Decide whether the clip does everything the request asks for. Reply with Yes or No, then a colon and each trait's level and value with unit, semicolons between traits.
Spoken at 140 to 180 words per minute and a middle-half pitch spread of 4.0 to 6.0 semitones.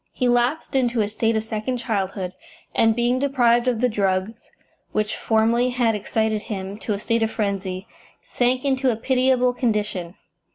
No: average, 165 wpm; average, 2.8 semitones